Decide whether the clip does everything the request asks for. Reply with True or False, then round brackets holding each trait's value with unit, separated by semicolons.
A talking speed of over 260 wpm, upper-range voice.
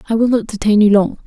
True (285 wpm; 215 Hz)